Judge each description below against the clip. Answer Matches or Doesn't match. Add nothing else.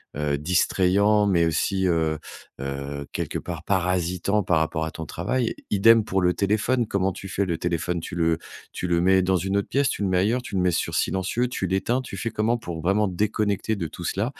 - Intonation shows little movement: Doesn't match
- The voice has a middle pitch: Doesn't match